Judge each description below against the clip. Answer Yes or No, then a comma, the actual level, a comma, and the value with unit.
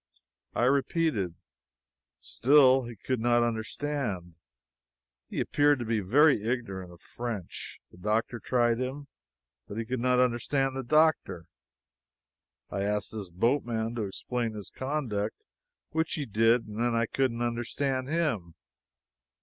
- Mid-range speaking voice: No, low, 120 Hz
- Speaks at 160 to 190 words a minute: No, slow, 135 wpm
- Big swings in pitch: No, average, 3.7 semitones